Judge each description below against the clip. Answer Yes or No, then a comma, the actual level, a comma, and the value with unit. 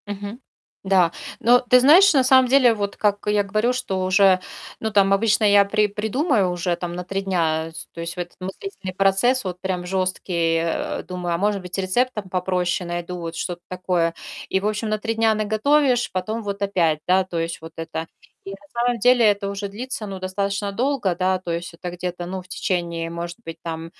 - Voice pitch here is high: Yes, high, 195 Hz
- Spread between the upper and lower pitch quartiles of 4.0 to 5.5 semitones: No, average, 3.3 semitones